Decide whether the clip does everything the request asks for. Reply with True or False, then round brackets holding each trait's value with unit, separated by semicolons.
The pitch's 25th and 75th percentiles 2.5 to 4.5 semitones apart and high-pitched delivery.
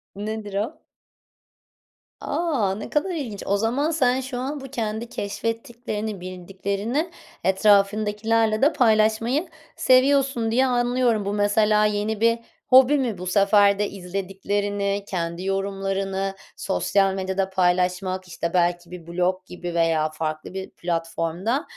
True (3.5 semitones; 205 Hz)